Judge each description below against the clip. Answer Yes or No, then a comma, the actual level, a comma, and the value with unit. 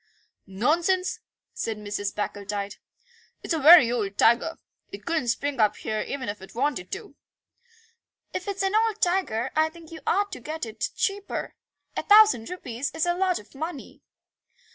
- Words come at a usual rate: Yes, average, 165 wpm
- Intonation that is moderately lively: No, wide, 8.3 semitones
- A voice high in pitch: Yes, very high, 285 Hz